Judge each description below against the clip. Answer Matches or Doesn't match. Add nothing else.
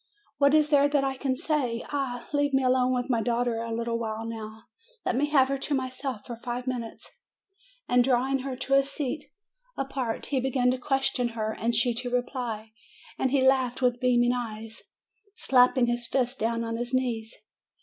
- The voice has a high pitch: Matches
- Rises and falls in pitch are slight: Matches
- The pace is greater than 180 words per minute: Matches